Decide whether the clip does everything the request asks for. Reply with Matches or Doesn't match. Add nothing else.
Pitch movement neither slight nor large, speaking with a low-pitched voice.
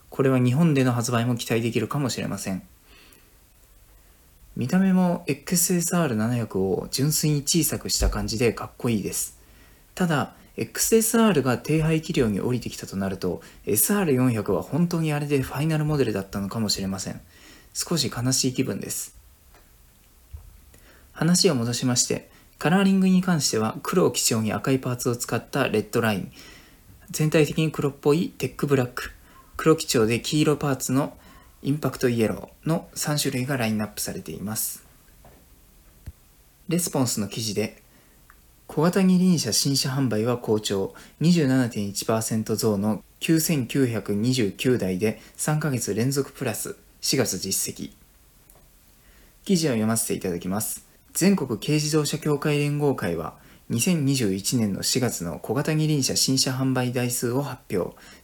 Doesn't match